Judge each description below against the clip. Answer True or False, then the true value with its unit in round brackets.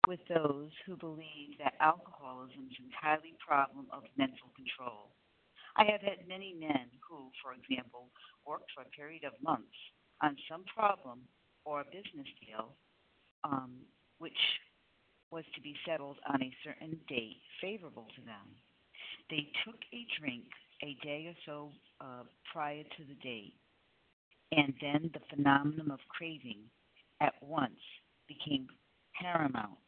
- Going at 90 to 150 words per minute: True (140 wpm)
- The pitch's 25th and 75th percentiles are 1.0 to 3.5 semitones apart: True (3.2 semitones)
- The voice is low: False (150 Hz)